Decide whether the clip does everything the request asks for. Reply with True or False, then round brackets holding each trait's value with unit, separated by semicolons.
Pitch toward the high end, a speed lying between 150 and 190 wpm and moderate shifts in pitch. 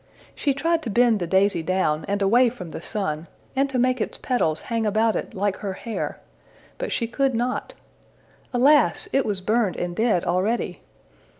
True (220 Hz; 180 wpm; 4.9 semitones)